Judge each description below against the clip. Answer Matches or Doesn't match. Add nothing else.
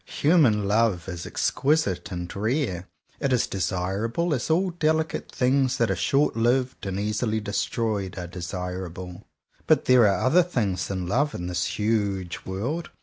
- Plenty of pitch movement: Matches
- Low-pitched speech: Matches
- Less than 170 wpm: Matches